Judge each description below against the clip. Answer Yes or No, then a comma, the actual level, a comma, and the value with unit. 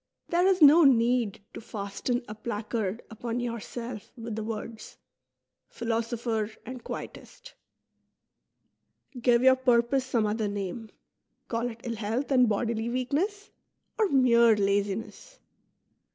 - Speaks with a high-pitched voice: Yes, high, 235 Hz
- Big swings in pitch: No, average, 2.7 semitones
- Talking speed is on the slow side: Yes, slow, 125 wpm